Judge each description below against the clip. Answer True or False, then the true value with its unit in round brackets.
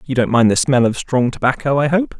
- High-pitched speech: False (135 Hz)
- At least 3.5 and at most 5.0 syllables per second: False (5.7 syllables/s)